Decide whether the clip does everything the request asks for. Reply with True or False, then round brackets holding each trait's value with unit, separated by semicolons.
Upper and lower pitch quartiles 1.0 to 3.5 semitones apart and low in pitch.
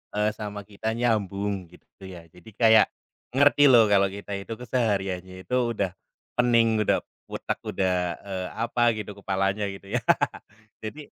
True (2.7 semitones; 105 Hz)